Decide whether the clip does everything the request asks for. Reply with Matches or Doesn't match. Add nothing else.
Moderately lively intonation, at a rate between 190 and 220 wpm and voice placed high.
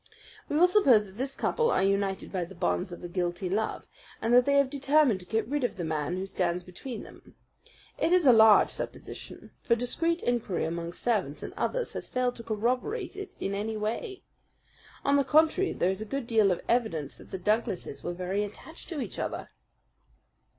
Doesn't match